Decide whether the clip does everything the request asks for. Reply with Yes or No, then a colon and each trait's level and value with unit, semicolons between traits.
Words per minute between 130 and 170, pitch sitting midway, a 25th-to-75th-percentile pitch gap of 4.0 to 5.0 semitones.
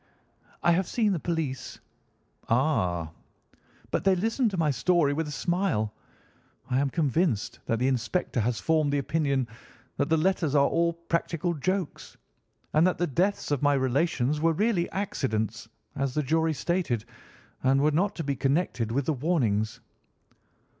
Yes: average, 160 wpm; medium, 150 Hz; average, 4.7 semitones